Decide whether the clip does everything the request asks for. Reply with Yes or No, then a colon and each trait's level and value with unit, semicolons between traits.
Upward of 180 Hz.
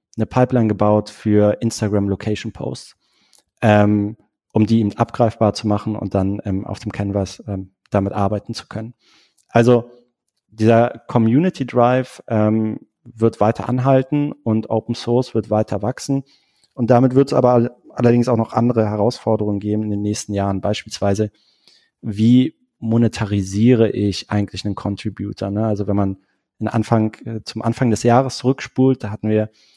No: low, 110 Hz